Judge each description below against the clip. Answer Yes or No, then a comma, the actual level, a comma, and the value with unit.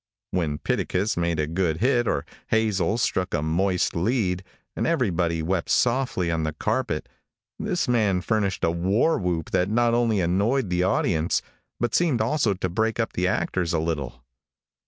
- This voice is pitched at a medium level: No, very low, 95 Hz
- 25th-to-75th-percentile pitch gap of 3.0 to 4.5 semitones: No, average, 5.1 semitones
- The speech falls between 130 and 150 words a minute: No, average, 165 wpm